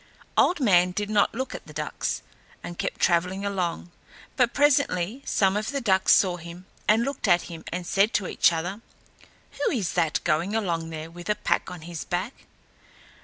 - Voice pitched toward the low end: No, medium, 185 Hz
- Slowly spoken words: No, average, 185 wpm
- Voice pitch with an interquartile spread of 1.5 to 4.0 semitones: Yes, average, 3.7 semitones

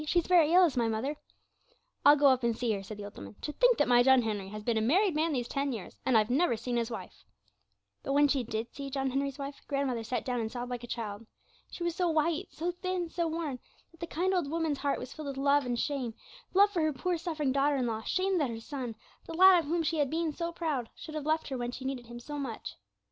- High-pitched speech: Yes, very high, 275 Hz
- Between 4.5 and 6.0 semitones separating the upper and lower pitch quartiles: Yes, average, 5.2 semitones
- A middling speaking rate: No, fast, 270 wpm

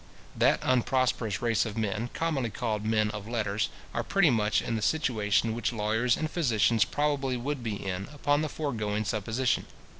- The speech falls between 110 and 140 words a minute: No, average, 170 wpm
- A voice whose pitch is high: No, low, 115 Hz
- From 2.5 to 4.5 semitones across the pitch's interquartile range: Yes, average, 3.6 semitones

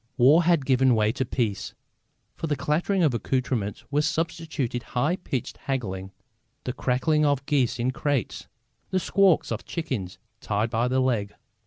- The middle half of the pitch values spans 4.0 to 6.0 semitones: Yes, average, 4.4 semitones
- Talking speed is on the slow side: No, average, 155 wpm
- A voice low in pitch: Yes, low, 130 Hz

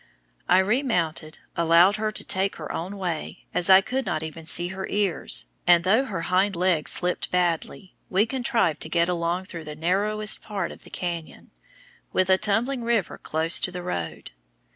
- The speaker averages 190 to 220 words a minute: No, average, 180 wpm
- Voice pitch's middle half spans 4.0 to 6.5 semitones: No, average, 3.4 semitones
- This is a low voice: No, medium, 185 Hz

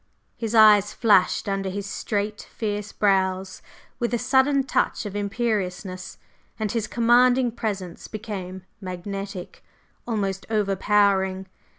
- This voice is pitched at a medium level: No, high, 205 Hz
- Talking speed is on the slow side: Yes, slow, 115 wpm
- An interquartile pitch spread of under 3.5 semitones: Yes, average, 2.7 semitones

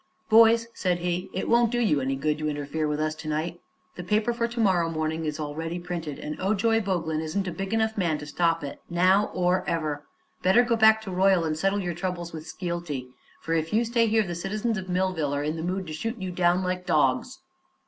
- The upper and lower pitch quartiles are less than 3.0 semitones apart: No, average, 4.3 semitones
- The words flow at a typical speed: No, fast, 230 wpm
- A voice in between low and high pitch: Yes, medium, 175 Hz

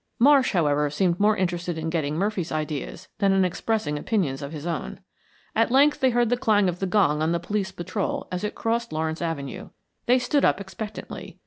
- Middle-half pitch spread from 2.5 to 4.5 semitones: No, average, 5.3 semitones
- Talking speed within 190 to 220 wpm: Yes, average, 200 wpm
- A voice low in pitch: No, medium, 185 Hz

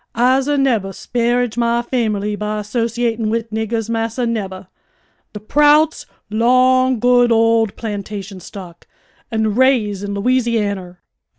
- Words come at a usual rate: No, slow, 115 wpm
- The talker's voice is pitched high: Yes, high, 225 Hz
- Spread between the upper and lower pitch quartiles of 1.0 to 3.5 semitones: Yes, average, 2.7 semitones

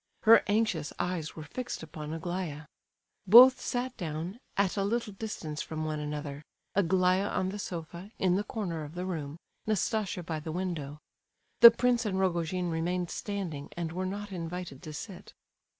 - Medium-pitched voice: Yes, medium, 180 Hz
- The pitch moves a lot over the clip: No, average, 4.0 semitones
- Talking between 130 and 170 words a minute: Yes, average, 160 wpm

